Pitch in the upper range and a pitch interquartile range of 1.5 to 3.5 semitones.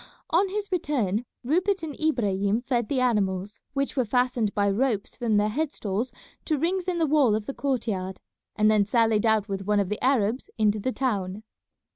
No: high, 230 Hz; average, 5.1 semitones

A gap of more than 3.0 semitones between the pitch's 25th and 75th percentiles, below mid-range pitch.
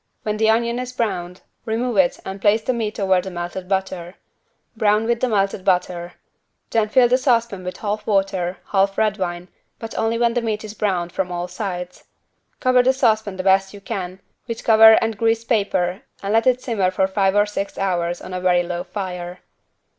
No: average, 3.5 semitones; high, 200 Hz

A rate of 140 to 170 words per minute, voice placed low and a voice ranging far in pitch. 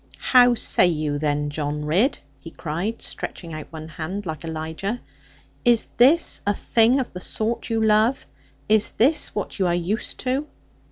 No: average, 165 wpm; high, 195 Hz; wide, 6.7 semitones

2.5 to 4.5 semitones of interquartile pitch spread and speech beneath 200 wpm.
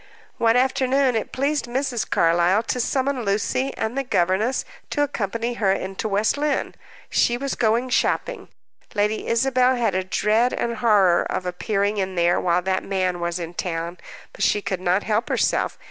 No: average, 5.0 semitones; average, 170 wpm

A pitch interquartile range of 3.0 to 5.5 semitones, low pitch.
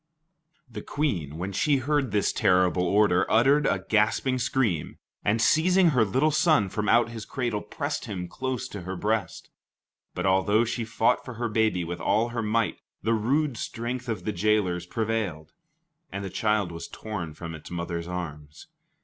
Yes: average, 5.1 semitones; low, 105 Hz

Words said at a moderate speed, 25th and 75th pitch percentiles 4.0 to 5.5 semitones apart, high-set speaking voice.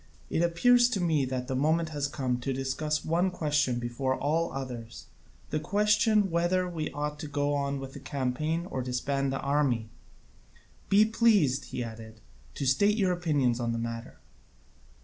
No: average, 170 wpm; average, 4.7 semitones; medium, 145 Hz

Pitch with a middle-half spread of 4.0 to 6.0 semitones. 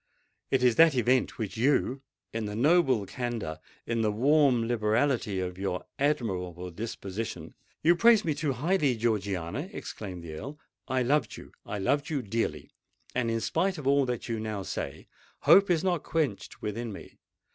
Yes: wide, 5.6 semitones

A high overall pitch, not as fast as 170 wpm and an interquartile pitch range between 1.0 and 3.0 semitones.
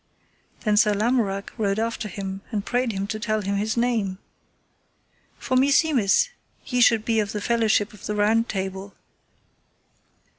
Yes: high, 215 Hz; average, 150 wpm; average, 2.7 semitones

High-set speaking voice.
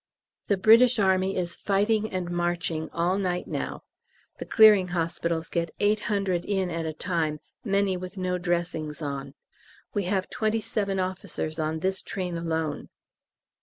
No: medium, 180 Hz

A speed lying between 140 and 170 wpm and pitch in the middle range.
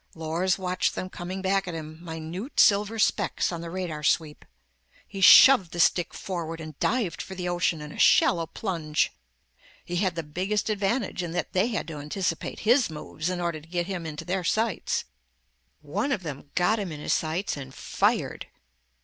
No: average, 185 wpm; medium, 175 Hz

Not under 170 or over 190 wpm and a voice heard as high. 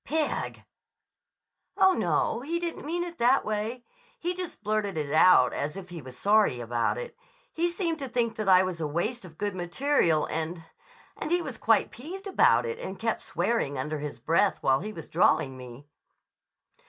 Yes: average, 180 wpm; high, 205 Hz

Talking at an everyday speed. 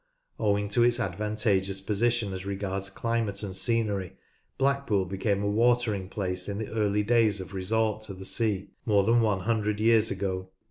Yes: average, 175 wpm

